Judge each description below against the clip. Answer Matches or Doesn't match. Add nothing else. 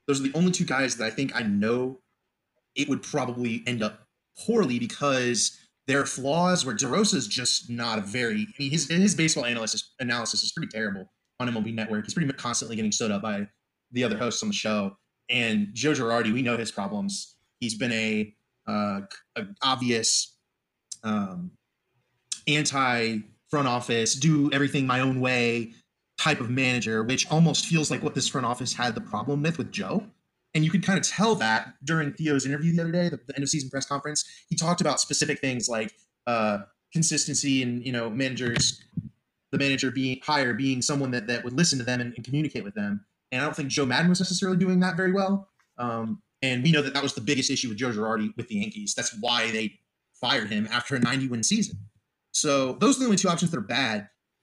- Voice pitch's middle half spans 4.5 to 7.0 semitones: Matches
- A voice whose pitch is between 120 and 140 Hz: Matches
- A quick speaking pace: Matches